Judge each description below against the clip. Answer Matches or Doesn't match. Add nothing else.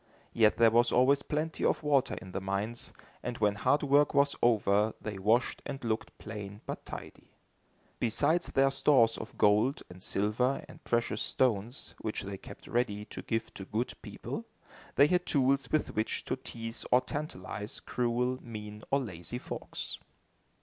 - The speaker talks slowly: Doesn't match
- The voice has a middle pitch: Doesn't match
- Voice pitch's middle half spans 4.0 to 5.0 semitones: Matches